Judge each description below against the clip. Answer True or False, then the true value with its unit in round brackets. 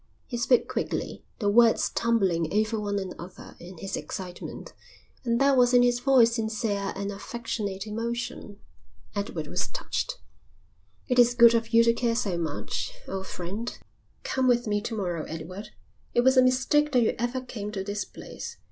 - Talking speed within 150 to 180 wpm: True (170 wpm)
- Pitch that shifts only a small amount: False (3.4 semitones)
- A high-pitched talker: True (225 Hz)